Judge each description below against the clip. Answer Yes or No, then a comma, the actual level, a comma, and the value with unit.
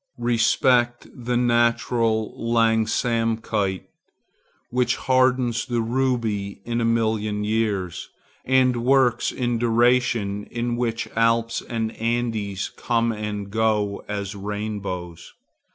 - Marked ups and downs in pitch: No, narrow, 2.4 semitones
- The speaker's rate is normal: No, slow, 95 wpm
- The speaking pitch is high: No, low, 115 Hz